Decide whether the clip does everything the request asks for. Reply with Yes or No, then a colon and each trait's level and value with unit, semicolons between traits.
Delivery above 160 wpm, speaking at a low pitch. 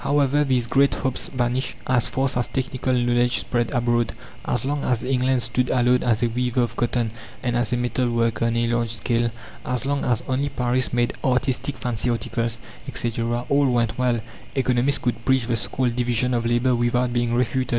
Yes: average, 190 wpm; low, 120 Hz